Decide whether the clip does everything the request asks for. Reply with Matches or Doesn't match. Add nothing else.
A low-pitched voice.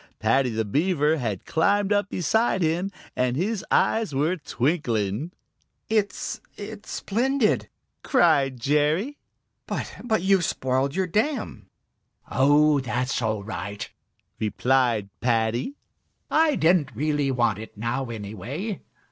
Doesn't match